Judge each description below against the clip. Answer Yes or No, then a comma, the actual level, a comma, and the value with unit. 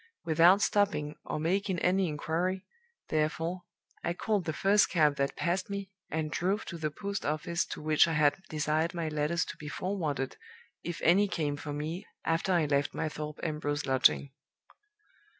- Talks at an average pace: Yes, average, 170 wpm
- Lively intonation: No, average, 3.4 semitones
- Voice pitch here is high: No, medium, 160 Hz